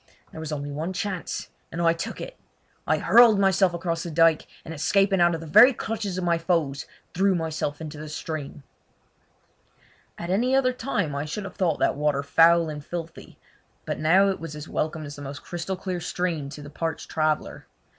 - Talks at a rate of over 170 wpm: Yes, average, 195 wpm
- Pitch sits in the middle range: Yes, medium, 165 Hz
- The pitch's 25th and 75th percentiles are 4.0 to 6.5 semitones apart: No, average, 3.6 semitones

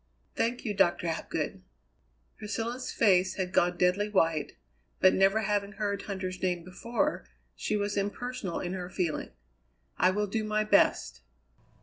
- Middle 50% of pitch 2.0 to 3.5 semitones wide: Yes, average, 2.7 semitones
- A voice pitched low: No, high, 195 Hz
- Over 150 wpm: No, average, 140 wpm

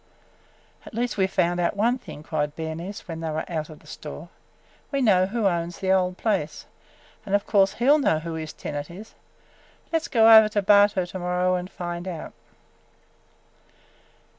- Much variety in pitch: No, average, 3.7 semitones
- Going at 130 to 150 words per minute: No, average, 190 wpm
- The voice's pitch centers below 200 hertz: Yes, medium, 185 Hz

